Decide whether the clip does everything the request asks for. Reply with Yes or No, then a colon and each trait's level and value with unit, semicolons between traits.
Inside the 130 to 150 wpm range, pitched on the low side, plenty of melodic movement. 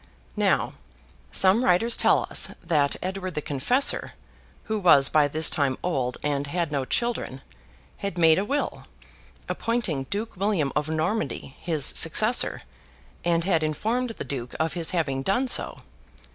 No: average, 145 wpm; medium, 170 Hz; wide, 6.2 semitones